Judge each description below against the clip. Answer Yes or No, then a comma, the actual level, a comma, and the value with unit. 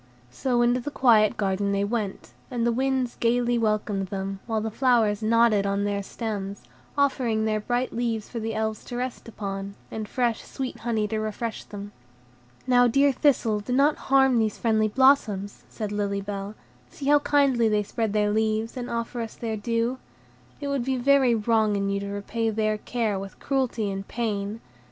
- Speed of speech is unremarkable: Yes, average, 185 wpm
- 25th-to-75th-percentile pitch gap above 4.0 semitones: No, average, 2.9 semitones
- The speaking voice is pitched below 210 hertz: No, high, 225 Hz